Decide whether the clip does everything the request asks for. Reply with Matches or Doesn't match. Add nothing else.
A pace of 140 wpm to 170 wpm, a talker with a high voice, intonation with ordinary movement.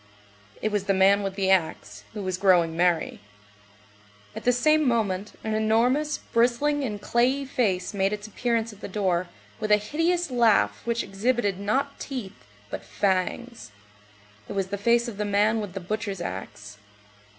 Matches